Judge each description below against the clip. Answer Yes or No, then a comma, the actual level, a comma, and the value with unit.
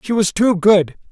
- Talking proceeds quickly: Yes, fast, 215 wpm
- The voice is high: Yes, high, 200 Hz